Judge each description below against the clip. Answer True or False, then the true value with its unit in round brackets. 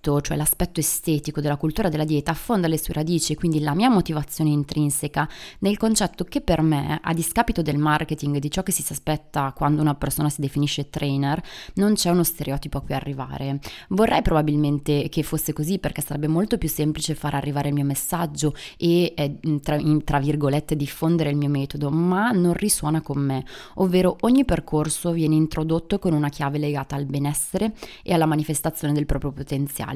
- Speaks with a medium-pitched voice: True (150 Hz)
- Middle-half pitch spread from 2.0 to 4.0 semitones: True (2.6 semitones)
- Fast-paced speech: True (175 wpm)